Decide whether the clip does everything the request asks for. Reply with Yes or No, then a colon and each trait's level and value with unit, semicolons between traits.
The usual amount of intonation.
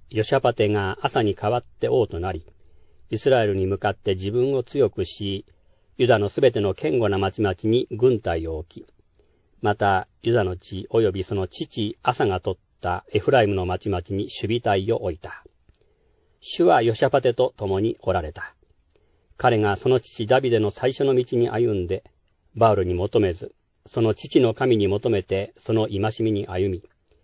Yes: average, 4.1 semitones